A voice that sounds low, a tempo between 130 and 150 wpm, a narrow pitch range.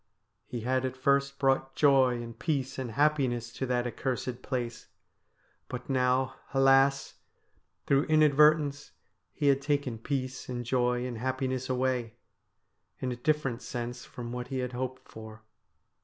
Yes: low, 130 Hz; average, 145 wpm; narrow, 1.9 semitones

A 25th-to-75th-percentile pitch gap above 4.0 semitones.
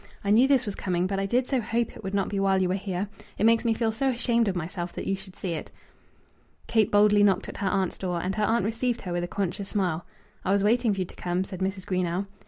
No: average, 3.1 semitones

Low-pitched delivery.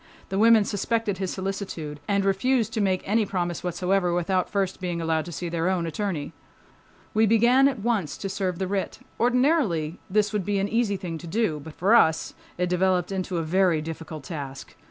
No: high, 190 Hz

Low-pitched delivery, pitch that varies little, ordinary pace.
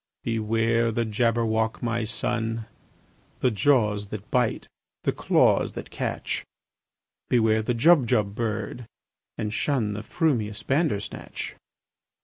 No: low, 115 Hz; narrow, 2.1 semitones; slow, 110 wpm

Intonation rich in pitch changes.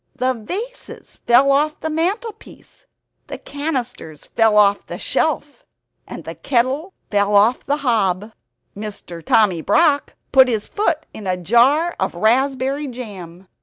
Yes: wide, 6.2 semitones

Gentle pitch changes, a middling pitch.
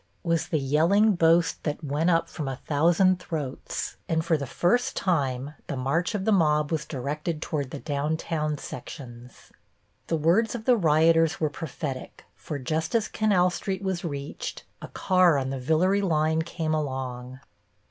No: average, 3.5 semitones; medium, 160 Hz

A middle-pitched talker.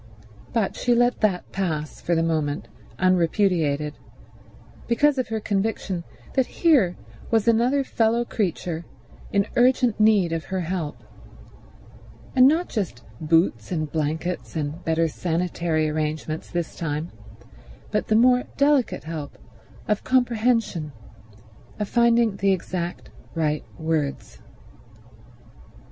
Yes: medium, 180 Hz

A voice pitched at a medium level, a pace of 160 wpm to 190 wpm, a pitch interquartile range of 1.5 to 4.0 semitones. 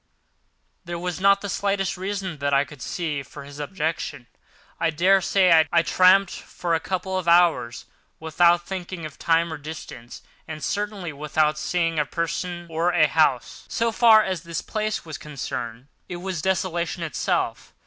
Yes: medium, 170 Hz; average, 165 wpm; average, 3.4 semitones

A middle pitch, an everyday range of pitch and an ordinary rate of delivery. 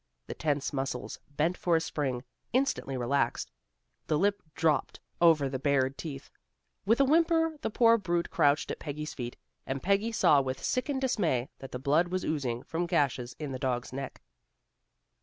No: medium, 150 Hz; wide, 6.1 semitones; average, 170 wpm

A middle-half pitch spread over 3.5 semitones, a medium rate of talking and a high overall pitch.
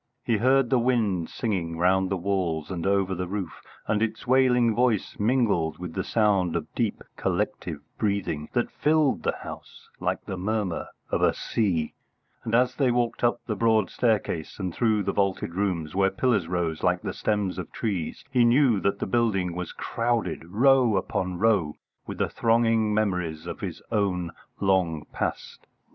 No: average, 4.4 semitones; average, 170 wpm; low, 100 Hz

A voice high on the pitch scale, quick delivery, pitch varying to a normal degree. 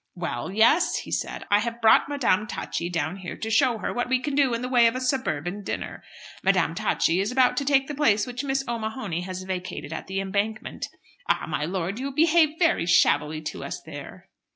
No: high, 220 Hz; fast, 210 wpm; wide, 6.1 semitones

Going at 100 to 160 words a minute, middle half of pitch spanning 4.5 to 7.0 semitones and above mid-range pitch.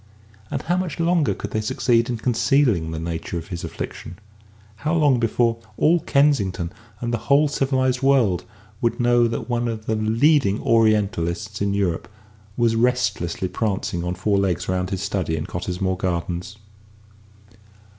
No: average, 155 wpm; wide, 5.4 semitones; low, 110 Hz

